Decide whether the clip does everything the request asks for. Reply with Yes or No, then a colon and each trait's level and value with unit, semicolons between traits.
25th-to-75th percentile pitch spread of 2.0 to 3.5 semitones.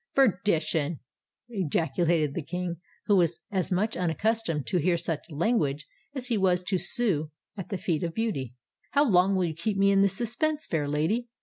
No: average, 4.6 semitones